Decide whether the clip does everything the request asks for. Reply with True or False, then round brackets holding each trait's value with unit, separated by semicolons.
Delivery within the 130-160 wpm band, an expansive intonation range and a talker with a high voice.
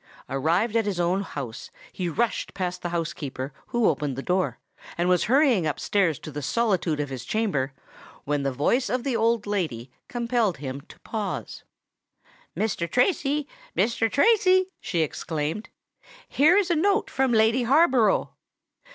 True (150 wpm; 7.9 semitones; 205 Hz)